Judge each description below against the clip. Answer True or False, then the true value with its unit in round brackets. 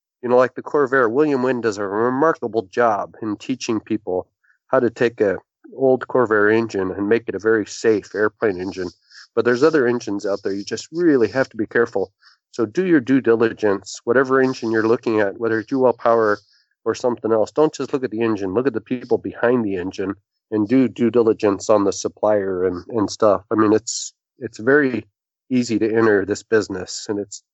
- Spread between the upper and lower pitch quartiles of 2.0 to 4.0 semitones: True (3.4 semitones)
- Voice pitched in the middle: False (115 Hz)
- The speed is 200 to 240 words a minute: True (205 wpm)